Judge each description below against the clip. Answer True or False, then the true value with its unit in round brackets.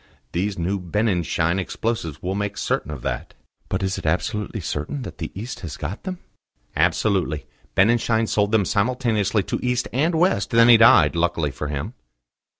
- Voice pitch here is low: True (100 Hz)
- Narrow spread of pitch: False (5.0 semitones)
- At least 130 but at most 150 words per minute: False (165 wpm)